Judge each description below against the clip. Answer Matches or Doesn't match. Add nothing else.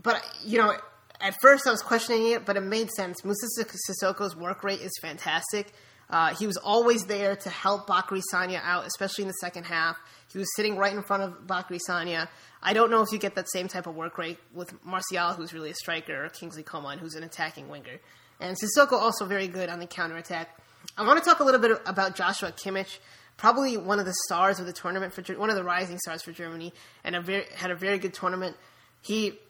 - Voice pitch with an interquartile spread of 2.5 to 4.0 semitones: Matches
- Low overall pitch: Doesn't match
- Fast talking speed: Matches